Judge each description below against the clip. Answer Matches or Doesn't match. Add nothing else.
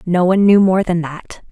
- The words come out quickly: Matches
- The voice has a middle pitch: Matches